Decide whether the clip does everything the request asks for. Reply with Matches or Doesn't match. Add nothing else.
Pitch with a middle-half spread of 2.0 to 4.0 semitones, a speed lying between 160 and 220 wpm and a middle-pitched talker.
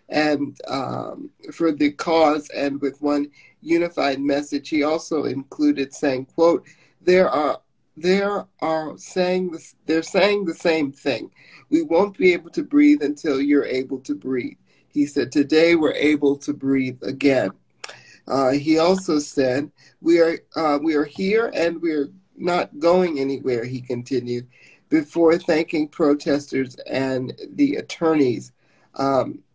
Doesn't match